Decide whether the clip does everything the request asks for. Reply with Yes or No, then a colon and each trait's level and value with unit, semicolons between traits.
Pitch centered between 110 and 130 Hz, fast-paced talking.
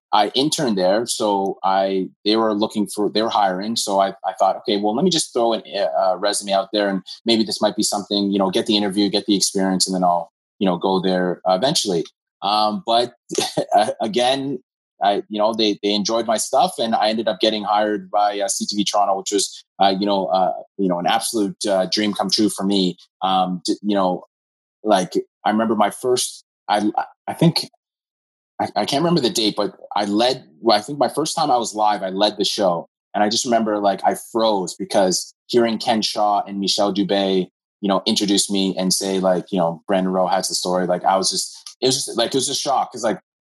No: low, 100 Hz; fast, 220 wpm